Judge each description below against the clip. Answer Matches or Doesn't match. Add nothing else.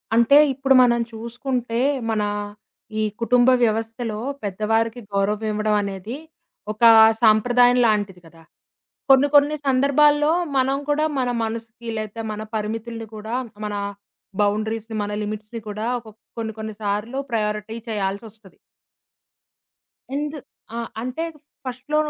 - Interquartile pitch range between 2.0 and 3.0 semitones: Matches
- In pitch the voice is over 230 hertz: Doesn't match